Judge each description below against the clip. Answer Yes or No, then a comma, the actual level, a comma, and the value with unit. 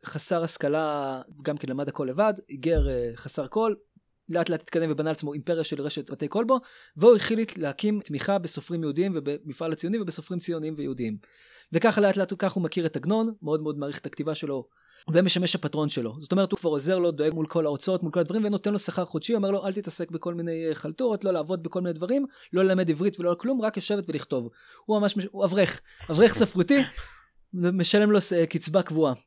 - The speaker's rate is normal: No, fast, 170 wpm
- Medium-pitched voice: Yes, medium, 170 Hz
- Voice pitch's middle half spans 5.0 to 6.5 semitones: No, average, 4.5 semitones